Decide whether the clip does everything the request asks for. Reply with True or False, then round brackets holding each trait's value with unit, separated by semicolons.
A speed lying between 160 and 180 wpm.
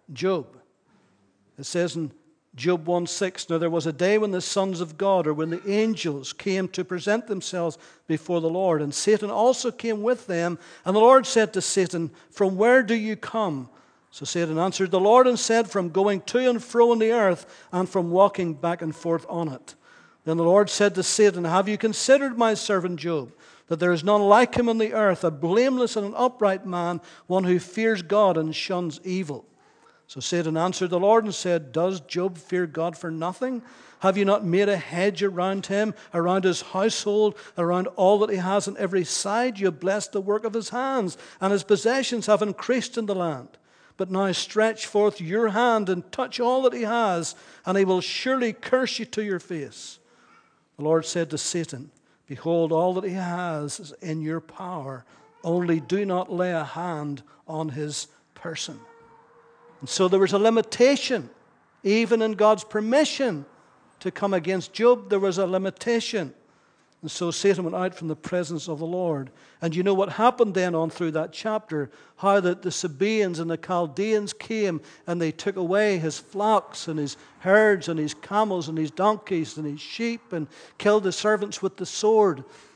False (195 wpm)